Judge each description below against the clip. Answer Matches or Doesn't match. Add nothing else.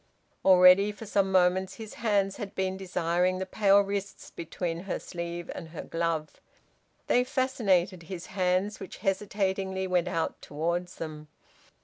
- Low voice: Doesn't match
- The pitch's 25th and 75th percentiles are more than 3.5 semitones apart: Doesn't match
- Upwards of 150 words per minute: Doesn't match